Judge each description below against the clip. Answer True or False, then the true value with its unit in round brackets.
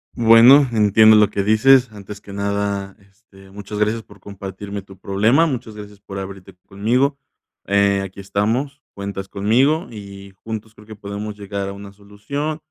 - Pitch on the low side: True (105 Hz)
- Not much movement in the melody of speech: True (2.1 semitones)